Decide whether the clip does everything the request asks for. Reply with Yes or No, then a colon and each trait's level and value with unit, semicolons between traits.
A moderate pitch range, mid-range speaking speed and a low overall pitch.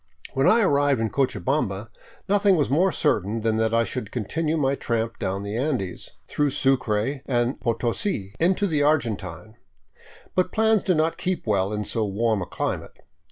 No: wide, 6.2 semitones; average, 165 wpm; low, 125 Hz